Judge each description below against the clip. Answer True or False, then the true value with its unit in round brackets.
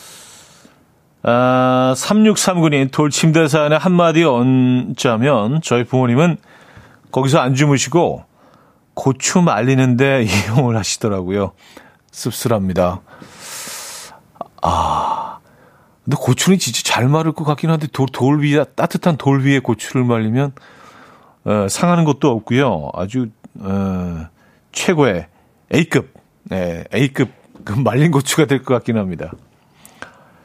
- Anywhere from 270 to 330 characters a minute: False (225 characters per minute)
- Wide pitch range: False (4.8 semitones)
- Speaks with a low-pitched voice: True (130 Hz)